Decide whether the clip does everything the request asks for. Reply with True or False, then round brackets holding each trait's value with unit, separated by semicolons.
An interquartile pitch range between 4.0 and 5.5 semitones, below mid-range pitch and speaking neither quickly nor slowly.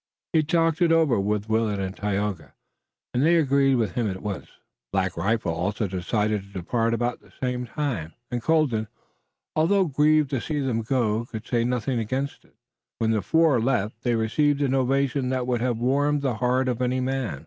True (4.4 semitones; 125 Hz; 190 wpm)